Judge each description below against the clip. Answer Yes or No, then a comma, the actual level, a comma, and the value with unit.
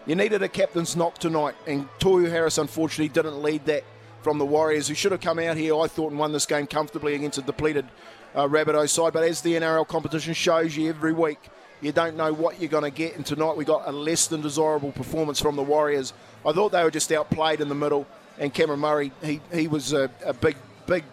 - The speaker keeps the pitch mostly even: Yes, narrow, 1.8 semitones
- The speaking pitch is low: No, medium, 155 Hz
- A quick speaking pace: Yes, fast, 235 wpm